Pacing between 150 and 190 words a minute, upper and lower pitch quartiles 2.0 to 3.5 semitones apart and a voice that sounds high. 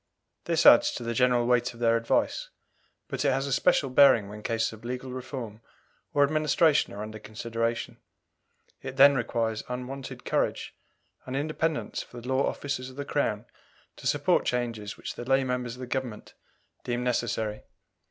No: average, 170 wpm; average, 2.7 semitones; low, 125 Hz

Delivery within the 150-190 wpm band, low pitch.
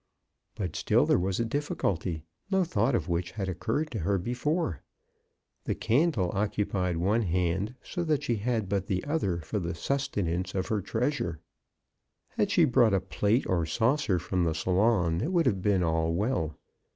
Yes: average, 175 wpm; low, 100 Hz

